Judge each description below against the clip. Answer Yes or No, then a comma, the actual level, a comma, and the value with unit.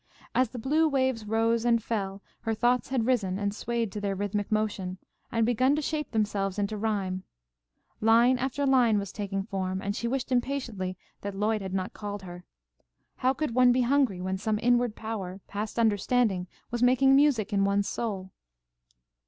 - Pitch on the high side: Yes, high, 220 Hz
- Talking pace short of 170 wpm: No, average, 175 wpm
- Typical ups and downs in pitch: Yes, average, 3.8 semitones